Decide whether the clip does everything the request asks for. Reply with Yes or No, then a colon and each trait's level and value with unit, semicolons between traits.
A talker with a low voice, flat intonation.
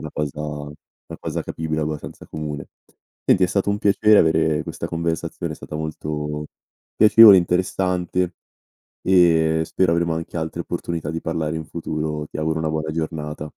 Yes: very low, 80 Hz; narrow, 2.0 semitones